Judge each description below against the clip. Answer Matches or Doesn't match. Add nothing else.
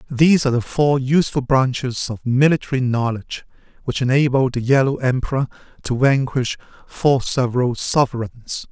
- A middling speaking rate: Doesn't match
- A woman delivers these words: Doesn't match